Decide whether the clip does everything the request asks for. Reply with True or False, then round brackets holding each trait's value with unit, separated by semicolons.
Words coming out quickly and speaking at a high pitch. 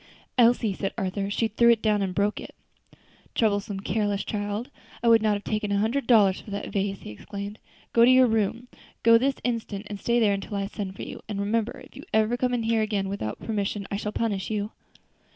True (220 wpm; 210 Hz)